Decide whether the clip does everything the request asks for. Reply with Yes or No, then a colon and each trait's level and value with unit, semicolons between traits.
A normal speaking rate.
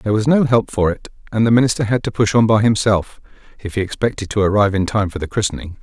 No: fast, 260 wpm